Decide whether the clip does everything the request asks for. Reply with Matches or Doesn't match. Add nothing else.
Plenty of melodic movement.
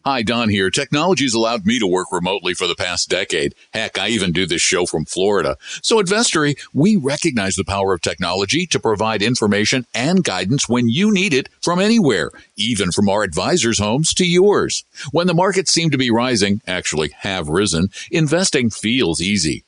Matches